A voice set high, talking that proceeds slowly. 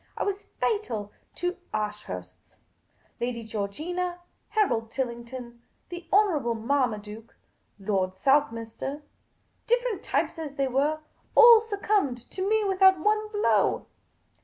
Yes: very high, 280 Hz; slow, 115 wpm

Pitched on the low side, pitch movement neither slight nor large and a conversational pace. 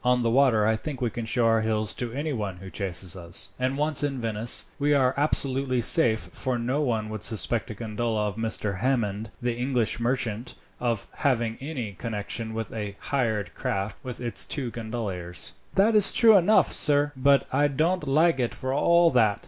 Yes: low, 120 Hz; average, 4.0 semitones; average, 190 wpm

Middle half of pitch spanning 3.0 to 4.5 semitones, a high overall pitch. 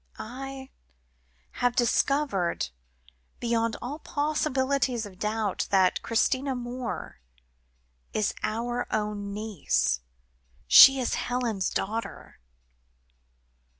Yes: average, 3.8 semitones; high, 235 Hz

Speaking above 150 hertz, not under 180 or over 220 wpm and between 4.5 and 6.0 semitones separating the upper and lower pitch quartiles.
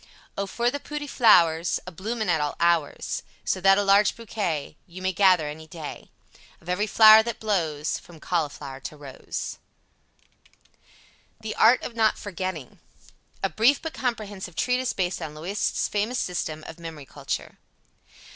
No: medium, 185 Hz; average, 155 wpm; wide, 5.4 semitones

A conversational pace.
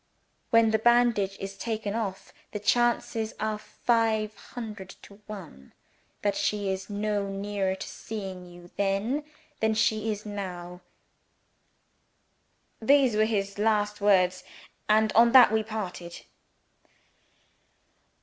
No: slow, 120 wpm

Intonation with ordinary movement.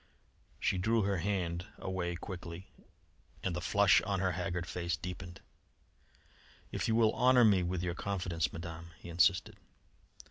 No: narrow, 2.3 semitones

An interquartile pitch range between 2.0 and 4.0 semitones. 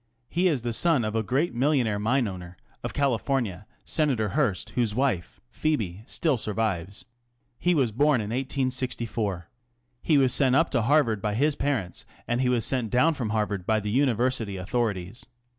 No: average, 4.5 semitones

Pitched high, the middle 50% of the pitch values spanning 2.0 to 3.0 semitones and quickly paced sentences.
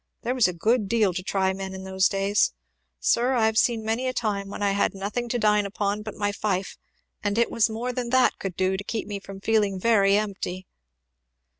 Yes: high, 205 Hz; average, 2.7 semitones; fast, 225 wpm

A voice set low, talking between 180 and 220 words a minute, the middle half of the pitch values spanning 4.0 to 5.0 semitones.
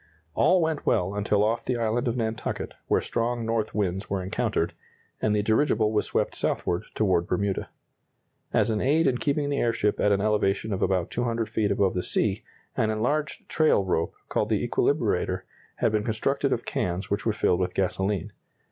No: low, 110 Hz; average, 185 wpm; average, 3.4 semitones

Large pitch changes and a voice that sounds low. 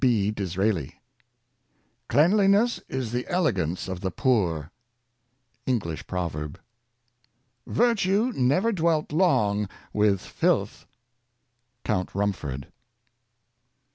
Yes: wide, 7.7 semitones; low, 120 Hz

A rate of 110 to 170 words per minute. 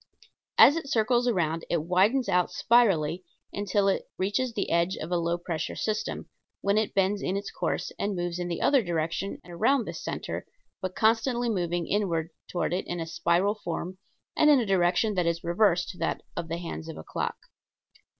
No: average, 190 wpm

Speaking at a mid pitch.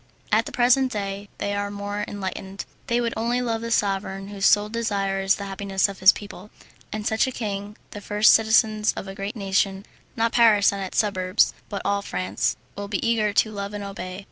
No: high, 205 Hz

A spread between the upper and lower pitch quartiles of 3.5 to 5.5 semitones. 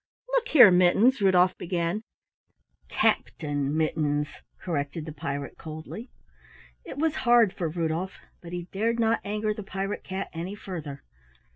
Yes: average, 5.0 semitones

